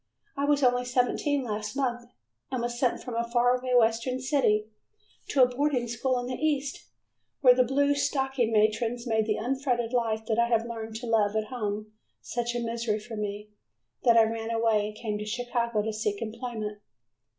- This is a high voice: Yes, high, 235 Hz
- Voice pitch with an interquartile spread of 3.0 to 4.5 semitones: No, narrow, 2.4 semitones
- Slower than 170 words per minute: No, average, 185 wpm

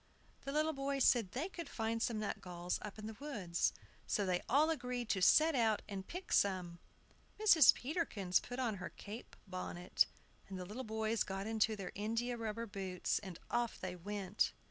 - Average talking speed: Yes, average, 180 wpm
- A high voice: Yes, high, 220 Hz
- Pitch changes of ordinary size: Yes, average, 4.6 semitones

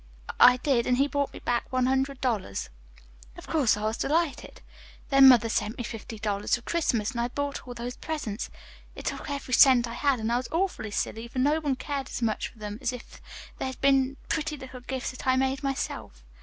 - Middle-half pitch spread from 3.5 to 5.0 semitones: No, average, 2.8 semitones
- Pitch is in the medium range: No, very high, 255 Hz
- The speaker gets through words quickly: Yes, fast, 215 wpm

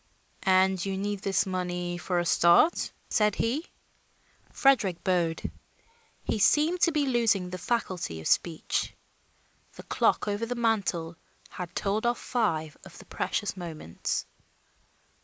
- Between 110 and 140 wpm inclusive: Yes, slow, 135 wpm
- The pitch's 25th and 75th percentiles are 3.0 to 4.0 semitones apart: No, average, 4.6 semitones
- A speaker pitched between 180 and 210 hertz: Yes, high, 190 Hz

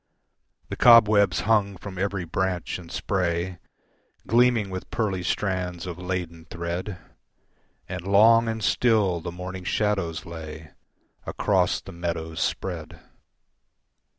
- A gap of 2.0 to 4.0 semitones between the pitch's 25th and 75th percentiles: Yes, average, 3.2 semitones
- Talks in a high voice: No, very low, 95 Hz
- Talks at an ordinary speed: No, slow, 115 wpm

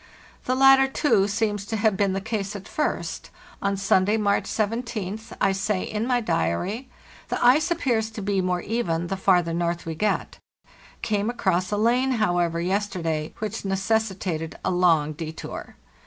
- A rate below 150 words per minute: No, average, 155 wpm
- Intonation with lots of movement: No, average, 3.7 semitones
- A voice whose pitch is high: Yes, high, 200 Hz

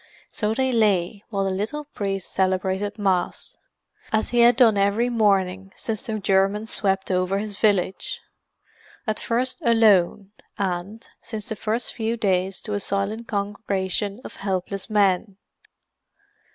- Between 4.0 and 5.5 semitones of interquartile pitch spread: No, narrow, 2.5 semitones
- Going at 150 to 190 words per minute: No, average, 140 wpm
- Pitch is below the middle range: No, high, 205 Hz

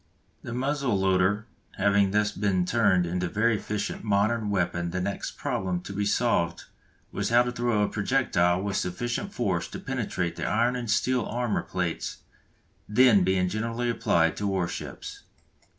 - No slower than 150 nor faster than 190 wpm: Yes, average, 165 wpm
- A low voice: Yes, low, 100 Hz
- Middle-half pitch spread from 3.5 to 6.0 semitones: Yes, average, 4.2 semitones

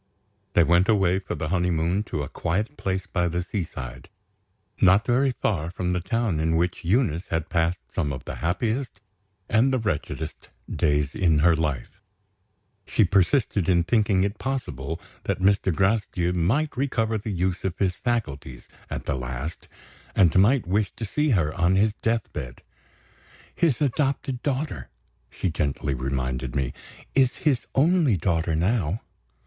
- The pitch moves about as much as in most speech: No, wide, 5.7 semitones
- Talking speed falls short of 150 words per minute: No, average, 155 wpm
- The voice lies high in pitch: No, very low, 95 Hz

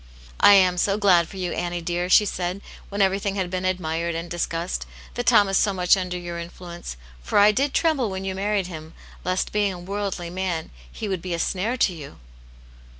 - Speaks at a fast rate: Yes, fast, 215 wpm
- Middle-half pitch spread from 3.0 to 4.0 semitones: No, narrow, 2.4 semitones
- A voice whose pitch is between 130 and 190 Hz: Yes, medium, 185 Hz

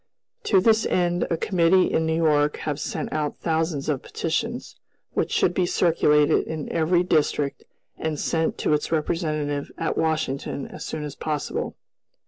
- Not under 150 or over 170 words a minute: Yes, average, 155 wpm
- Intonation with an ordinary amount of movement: No, narrow, 2.3 semitones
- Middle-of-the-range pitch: Yes, medium, 160 Hz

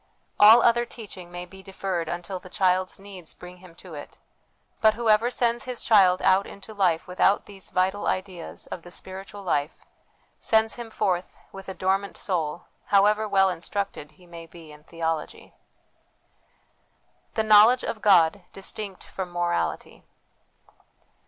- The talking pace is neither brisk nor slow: Yes, average, 150 wpm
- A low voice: No, high, 190 Hz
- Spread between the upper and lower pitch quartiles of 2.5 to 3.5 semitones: Yes, average, 2.8 semitones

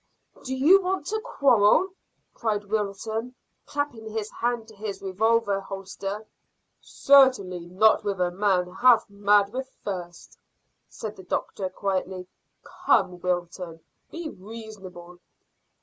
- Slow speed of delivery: Yes, slow, 120 wpm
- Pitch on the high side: Yes, high, 205 Hz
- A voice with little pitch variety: No, average, 3.7 semitones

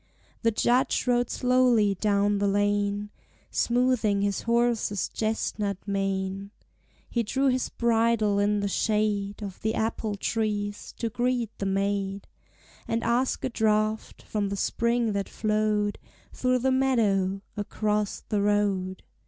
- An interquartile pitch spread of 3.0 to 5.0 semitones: No, narrow, 2.5 semitones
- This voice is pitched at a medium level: No, high, 210 Hz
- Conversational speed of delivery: No, slow, 130 wpm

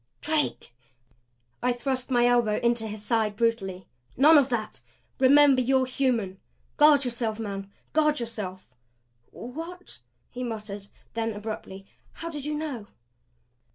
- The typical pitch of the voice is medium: No, high, 240 Hz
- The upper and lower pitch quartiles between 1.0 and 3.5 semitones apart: No, average, 4.3 semitones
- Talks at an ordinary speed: No, slow, 125 wpm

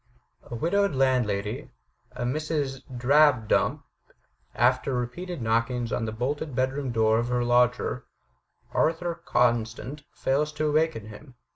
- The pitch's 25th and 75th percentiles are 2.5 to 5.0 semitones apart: Yes, average, 4.1 semitones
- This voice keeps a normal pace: No, slow, 120 wpm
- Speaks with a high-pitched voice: No, low, 130 Hz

